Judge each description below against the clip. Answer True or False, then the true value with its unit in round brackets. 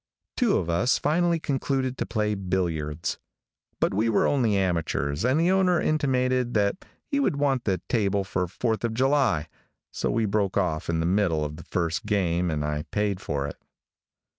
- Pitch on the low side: True (105 Hz)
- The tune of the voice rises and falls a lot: True (7.2 semitones)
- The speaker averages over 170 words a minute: True (180 wpm)